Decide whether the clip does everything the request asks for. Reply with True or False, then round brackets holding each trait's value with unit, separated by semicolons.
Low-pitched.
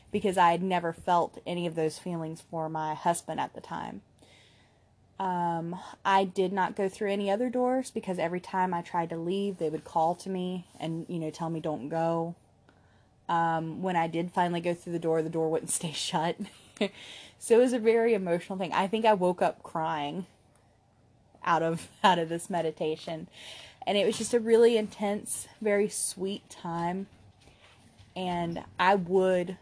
False (175 Hz)